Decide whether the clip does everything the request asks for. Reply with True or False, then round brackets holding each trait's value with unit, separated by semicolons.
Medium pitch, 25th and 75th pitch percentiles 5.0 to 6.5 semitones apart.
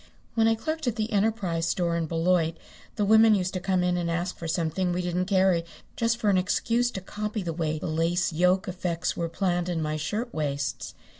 False (180 Hz; 3.8 semitones)